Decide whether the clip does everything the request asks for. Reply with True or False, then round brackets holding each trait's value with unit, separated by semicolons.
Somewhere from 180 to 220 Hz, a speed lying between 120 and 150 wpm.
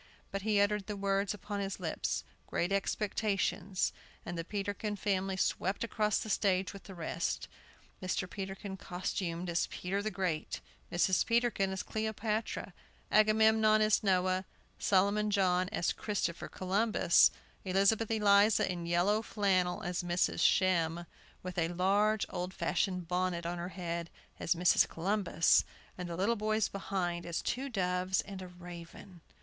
True (190 Hz; 145 wpm)